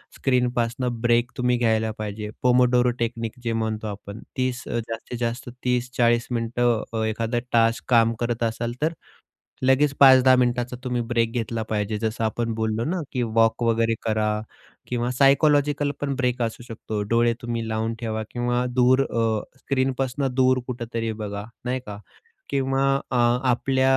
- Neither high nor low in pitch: No, low, 120 Hz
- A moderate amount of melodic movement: No, narrow, 1.9 semitones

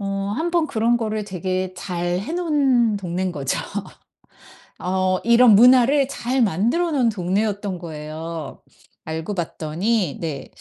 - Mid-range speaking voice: No, high, 200 Hz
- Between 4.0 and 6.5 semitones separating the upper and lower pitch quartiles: Yes, average, 5.3 semitones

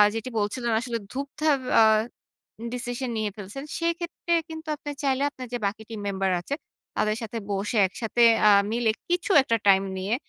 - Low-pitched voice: No, high, 235 Hz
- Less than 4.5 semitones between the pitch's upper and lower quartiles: No, average, 4.8 semitones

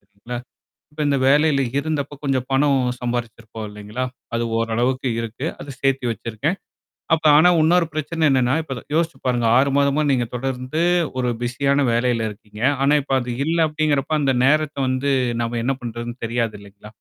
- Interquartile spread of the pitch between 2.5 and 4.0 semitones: Yes, average, 3.4 semitones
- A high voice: No, low, 130 Hz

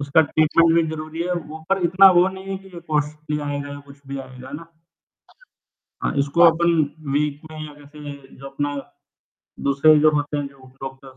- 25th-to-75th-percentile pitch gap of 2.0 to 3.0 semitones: Yes, narrow, 2.6 semitones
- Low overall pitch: No, medium, 150 Hz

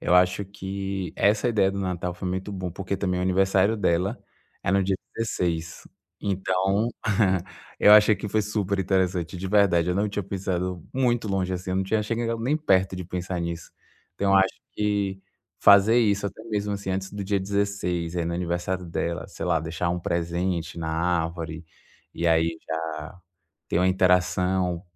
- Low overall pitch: Yes, very low, 95 Hz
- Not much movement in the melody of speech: Yes, narrow, 2.3 semitones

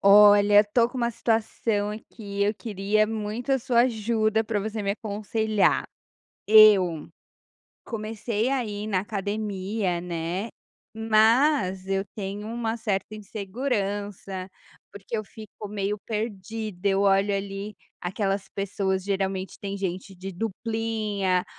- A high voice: Yes, high, 205 Hz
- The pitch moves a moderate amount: No, narrow, 2.2 semitones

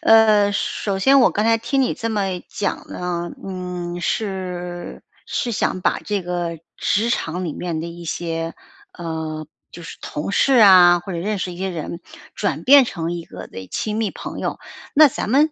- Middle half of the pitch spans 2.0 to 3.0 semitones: No, average, 3.8 semitones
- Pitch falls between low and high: Yes, medium, 180 Hz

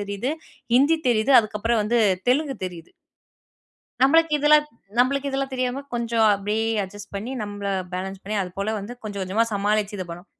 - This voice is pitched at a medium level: No, high, 220 Hz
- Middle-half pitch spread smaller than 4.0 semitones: No, average, 4.6 semitones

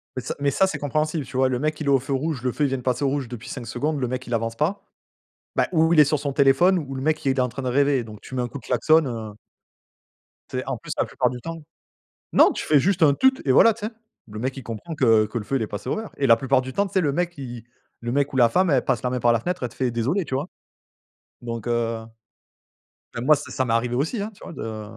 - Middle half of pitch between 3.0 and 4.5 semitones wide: Yes, average, 4.0 semitones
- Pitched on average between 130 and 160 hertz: Yes, low, 135 Hz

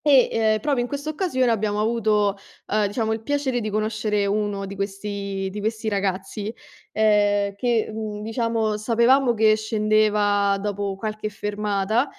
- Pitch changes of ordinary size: No, narrow, 1.8 semitones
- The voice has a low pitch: No, high, 215 Hz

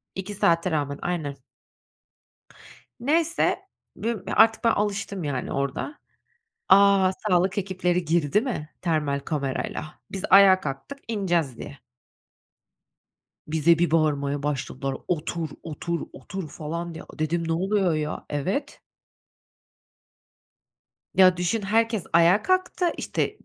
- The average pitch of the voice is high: No, medium, 175 Hz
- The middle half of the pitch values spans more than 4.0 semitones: Yes, average, 4.8 semitones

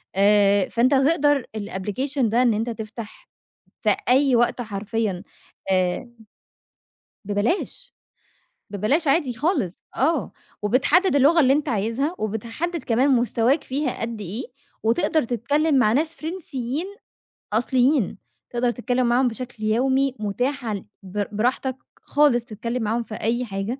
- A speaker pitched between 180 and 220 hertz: No, high, 240 Hz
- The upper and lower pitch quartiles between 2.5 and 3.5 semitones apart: No, average, 4.2 semitones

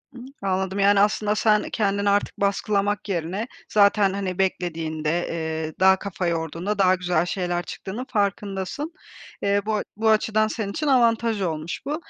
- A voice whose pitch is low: No, high, 200 Hz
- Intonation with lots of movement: No, average, 2.8 semitones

